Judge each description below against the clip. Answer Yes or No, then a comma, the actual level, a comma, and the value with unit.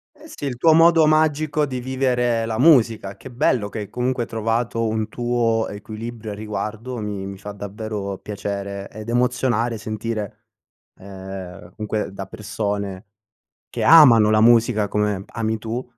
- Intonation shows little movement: No, average, 3.1 semitones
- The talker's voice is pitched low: Yes, low, 110 Hz